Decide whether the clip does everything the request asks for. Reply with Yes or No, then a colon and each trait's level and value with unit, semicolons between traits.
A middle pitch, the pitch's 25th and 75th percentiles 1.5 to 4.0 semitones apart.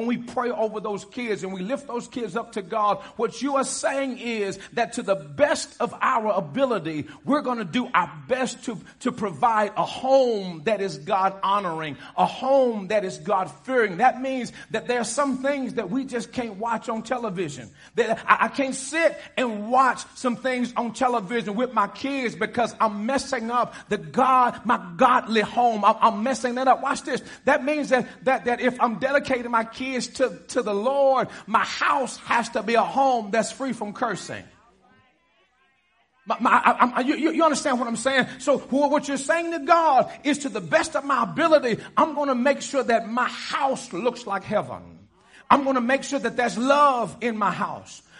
No: high, 245 Hz; average, 3.5 semitones